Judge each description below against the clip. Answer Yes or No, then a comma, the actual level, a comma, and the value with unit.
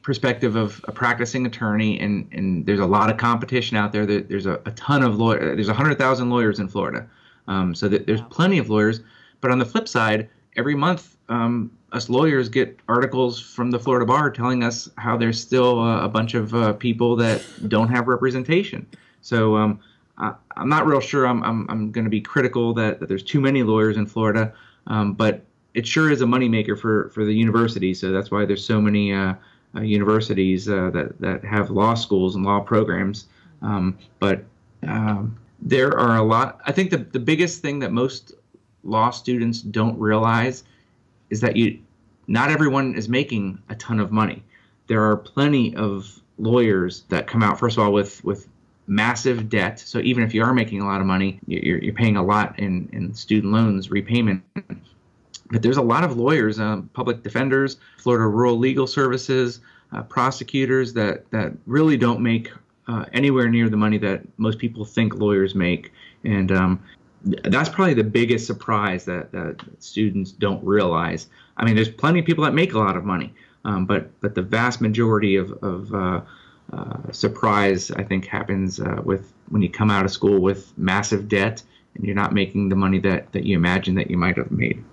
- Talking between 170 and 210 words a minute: Yes, average, 195 wpm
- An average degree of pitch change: Yes, average, 3.2 semitones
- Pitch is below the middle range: Yes, low, 110 Hz